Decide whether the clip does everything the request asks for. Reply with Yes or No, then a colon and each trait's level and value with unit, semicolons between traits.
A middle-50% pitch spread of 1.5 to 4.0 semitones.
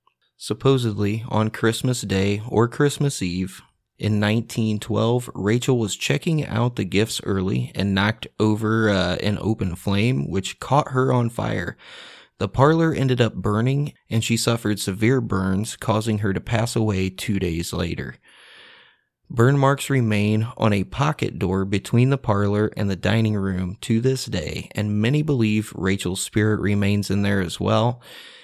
Yes: average, 3.4 semitones